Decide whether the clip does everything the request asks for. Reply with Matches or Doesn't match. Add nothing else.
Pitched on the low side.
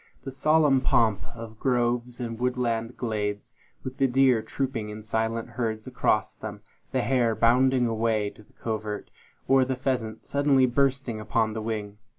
Matches